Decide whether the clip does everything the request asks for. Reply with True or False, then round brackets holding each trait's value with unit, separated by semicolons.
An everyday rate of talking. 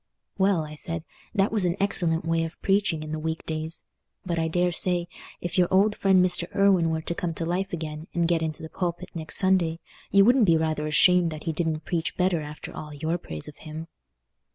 False (210 wpm)